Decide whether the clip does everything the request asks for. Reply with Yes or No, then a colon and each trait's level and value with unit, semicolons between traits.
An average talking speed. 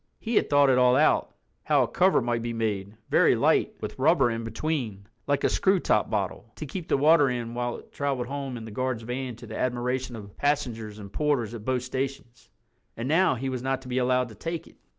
No: fast, 220 wpm